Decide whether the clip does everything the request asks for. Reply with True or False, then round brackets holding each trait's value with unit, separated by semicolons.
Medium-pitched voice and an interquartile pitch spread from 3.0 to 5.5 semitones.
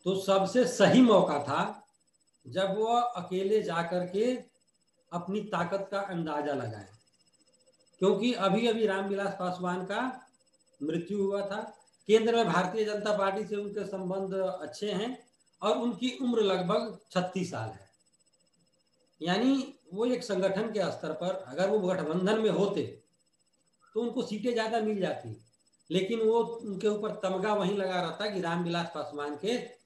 False (200 Hz; 3.5 semitones)